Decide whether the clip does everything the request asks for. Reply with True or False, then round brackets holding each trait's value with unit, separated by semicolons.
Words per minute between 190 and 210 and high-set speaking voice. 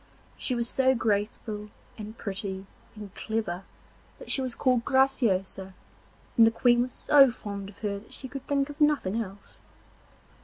False (160 wpm; 225 Hz)